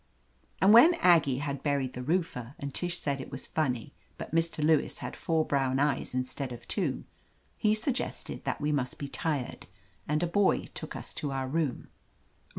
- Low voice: No, medium, 145 Hz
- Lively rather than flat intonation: No, average, 3.8 semitones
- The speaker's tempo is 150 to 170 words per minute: No, average, 180 wpm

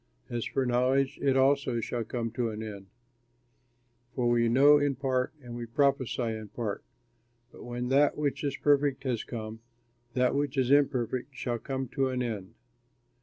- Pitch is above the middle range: No, low, 125 Hz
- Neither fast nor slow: Yes, average, 170 wpm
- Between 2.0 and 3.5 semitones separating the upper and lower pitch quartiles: Yes, narrow, 2.6 semitones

